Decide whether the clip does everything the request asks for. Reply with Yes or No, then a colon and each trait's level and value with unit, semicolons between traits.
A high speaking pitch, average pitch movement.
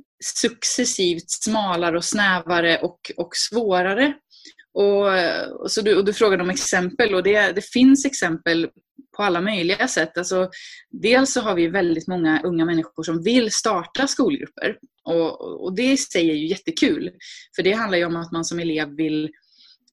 No: high, 195 Hz; wide, 6.8 semitones